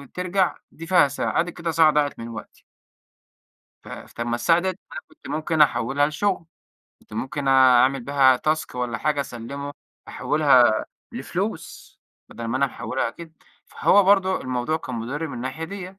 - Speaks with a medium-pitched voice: Yes, medium, 145 Hz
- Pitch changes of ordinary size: Yes, average, 4.5 semitones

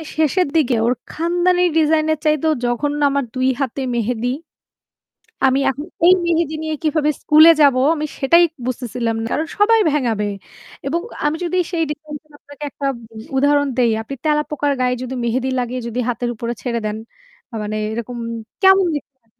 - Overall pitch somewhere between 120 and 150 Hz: No, very high, 285 Hz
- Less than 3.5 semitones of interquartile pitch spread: No, average, 4.1 semitones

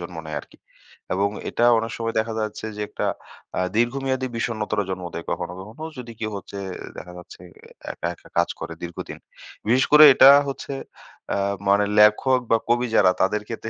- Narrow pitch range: No, average, 3.5 semitones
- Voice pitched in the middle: No, low, 110 Hz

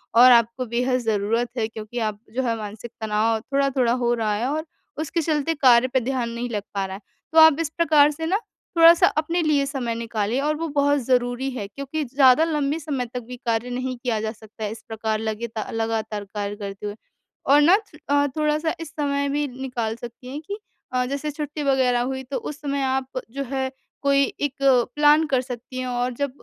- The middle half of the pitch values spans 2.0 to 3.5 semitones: No, average, 3.9 semitones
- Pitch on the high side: Yes, very high, 255 Hz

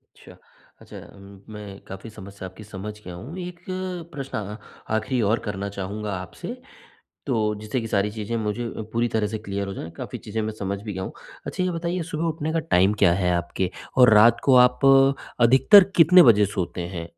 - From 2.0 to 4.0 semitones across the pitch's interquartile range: No, average, 4.4 semitones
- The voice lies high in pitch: No, low, 105 Hz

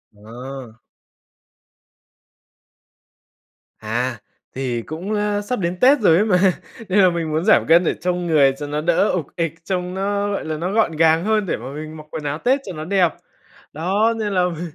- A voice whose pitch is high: No, medium, 170 Hz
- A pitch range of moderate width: Yes, average, 4.7 semitones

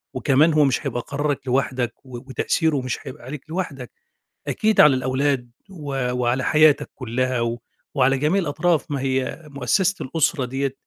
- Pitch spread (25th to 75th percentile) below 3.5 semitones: Yes, average, 2.9 semitones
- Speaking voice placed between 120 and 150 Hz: Yes, low, 135 Hz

